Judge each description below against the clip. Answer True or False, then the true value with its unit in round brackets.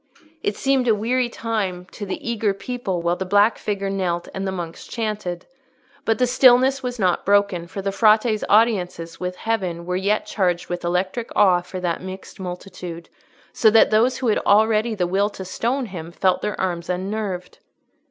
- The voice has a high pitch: True (195 Hz)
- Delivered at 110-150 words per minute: False (180 wpm)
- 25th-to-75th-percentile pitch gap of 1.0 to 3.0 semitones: False (3.7 semitones)